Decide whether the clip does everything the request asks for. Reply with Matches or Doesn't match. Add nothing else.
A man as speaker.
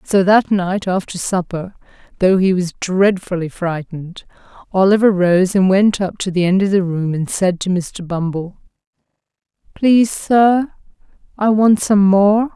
Doesn't match